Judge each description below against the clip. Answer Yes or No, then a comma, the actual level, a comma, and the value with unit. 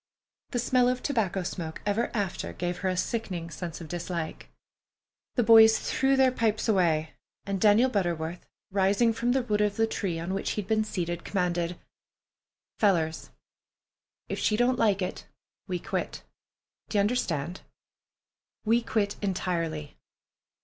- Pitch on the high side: Yes, high, 195 Hz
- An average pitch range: Yes, average, 4.4 semitones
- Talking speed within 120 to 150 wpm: Yes, average, 145 wpm